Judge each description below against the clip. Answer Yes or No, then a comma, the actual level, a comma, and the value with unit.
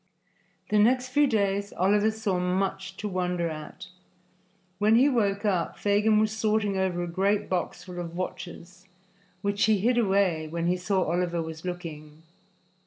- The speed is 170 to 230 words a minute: No, average, 160 wpm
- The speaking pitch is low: No, high, 190 Hz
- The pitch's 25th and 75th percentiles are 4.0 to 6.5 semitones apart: No, average, 3.0 semitones